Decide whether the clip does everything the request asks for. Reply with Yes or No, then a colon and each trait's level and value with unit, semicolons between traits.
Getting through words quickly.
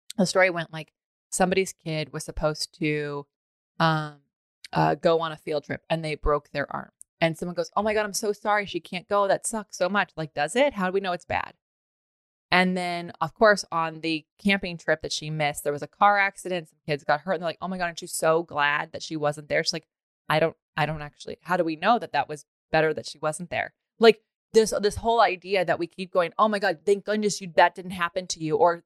Yes: fast, 250 wpm